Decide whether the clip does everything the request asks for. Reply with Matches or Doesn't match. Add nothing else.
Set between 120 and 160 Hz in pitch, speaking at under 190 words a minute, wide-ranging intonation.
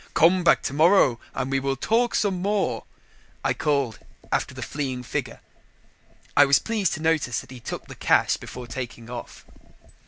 Matches